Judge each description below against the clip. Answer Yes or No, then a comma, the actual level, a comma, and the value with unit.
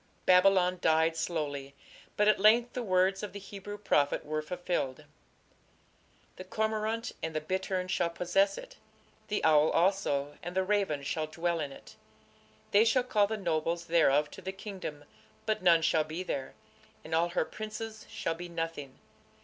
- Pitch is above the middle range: No, medium, 180 Hz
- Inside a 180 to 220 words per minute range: No, average, 165 wpm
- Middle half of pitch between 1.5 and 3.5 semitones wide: No, average, 4.2 semitones